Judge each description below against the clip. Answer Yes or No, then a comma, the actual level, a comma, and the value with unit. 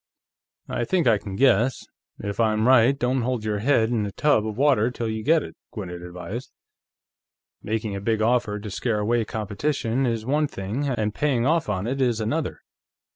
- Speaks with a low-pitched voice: Yes, low, 115 Hz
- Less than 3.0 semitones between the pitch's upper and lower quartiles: No, average, 3.7 semitones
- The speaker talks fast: No, average, 185 wpm